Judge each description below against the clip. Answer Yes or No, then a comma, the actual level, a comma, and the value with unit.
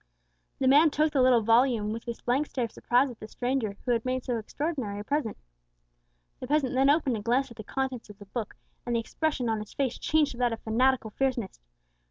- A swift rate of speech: Yes, fast, 230 wpm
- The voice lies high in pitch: Yes, very high, 250 Hz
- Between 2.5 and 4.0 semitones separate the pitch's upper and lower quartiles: Yes, average, 3.1 semitones